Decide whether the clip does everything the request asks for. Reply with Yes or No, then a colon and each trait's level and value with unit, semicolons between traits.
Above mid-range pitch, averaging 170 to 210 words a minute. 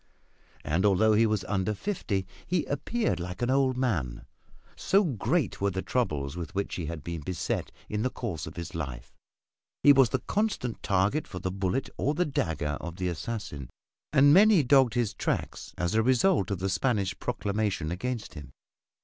No: low, 100 Hz; average, 180 wpm